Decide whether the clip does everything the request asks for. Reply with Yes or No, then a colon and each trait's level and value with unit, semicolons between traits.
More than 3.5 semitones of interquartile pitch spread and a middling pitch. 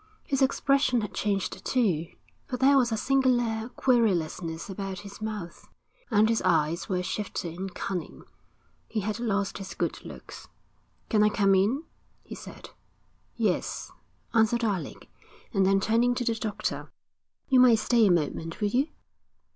No: average, 3.9 semitones; high, 215 Hz